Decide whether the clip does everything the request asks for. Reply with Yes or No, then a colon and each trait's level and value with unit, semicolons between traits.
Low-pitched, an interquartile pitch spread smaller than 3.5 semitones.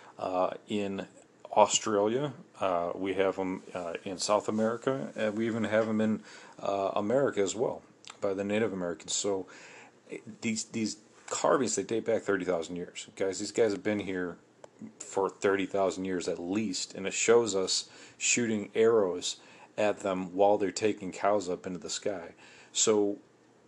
Yes: low, 100 Hz; narrow, 2.4 semitones